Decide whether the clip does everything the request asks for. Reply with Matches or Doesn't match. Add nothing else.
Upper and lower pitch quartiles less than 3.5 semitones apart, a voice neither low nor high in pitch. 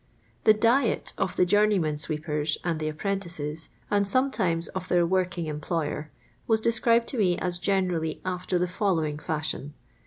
Doesn't match